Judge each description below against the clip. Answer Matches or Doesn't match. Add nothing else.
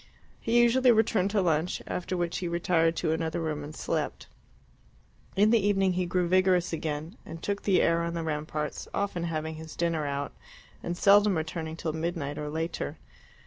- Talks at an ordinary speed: Matches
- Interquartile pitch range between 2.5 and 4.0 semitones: Matches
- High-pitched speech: Doesn't match